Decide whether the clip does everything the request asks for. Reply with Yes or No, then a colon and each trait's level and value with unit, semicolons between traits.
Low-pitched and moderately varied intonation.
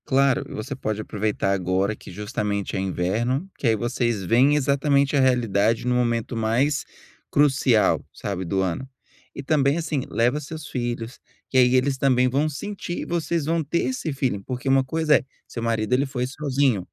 Yes: low, 130 Hz; average, 4.3 semitones